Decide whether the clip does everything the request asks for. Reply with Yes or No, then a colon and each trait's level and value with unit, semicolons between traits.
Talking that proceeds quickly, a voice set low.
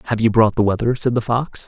Yes: fast, 285 wpm; low, 115 Hz